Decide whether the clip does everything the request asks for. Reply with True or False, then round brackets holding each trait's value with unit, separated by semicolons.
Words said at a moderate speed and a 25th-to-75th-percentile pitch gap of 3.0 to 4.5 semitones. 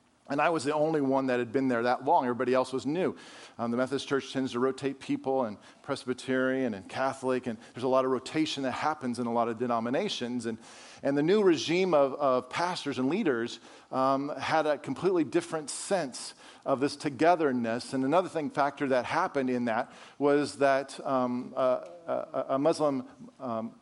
False (190 wpm; 2.4 semitones)